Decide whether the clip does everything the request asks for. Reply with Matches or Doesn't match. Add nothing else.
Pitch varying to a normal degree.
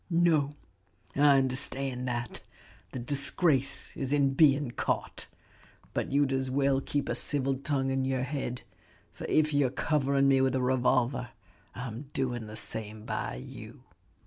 Doesn't match